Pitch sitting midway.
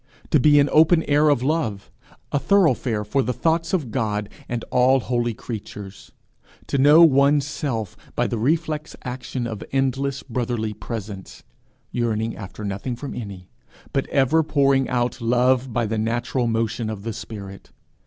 No: low, 125 Hz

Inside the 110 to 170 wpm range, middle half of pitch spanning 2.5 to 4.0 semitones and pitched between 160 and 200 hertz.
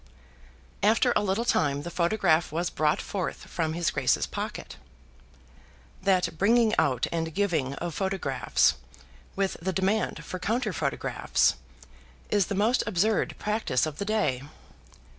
No: slow, 135 wpm; average, 4.7 semitones; medium, 185 Hz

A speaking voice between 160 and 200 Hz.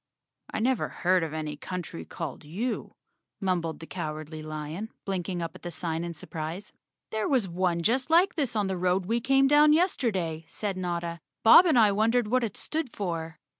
Yes: medium, 185 Hz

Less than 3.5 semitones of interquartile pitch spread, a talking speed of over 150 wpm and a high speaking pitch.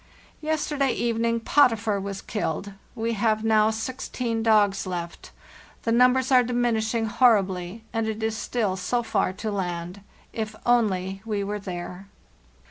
No: average, 3.0 semitones; average, 145 wpm; high, 220 Hz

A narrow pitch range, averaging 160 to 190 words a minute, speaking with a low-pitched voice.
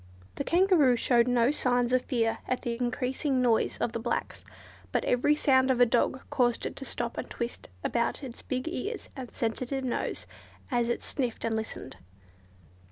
No: narrow, 2.0 semitones; average, 175 wpm; very high, 250 Hz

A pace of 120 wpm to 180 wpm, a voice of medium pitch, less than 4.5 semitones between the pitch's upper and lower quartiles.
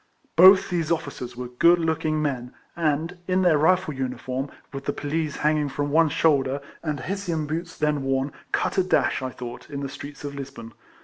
No: average, 200 wpm; medium, 150 Hz; average, 3.5 semitones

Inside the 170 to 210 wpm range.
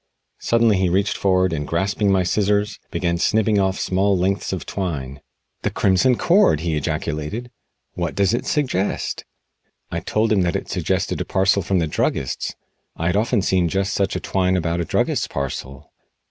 Yes: average, 175 wpm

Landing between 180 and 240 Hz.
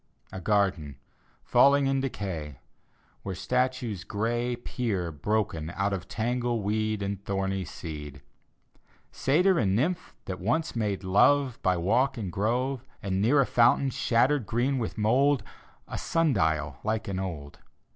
No: low, 110 Hz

